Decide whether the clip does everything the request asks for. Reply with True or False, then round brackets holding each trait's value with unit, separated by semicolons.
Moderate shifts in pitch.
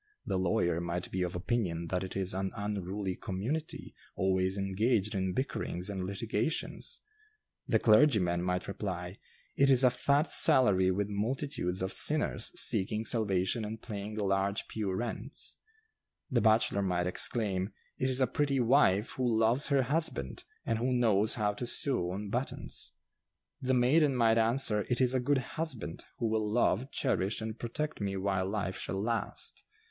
True (4.6 semitones)